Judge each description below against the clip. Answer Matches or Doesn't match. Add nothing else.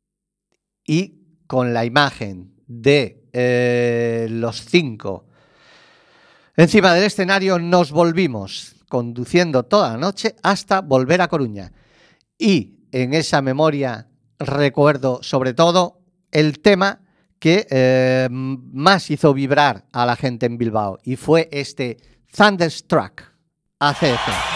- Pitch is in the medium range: Matches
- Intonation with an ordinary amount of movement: Doesn't match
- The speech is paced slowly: Matches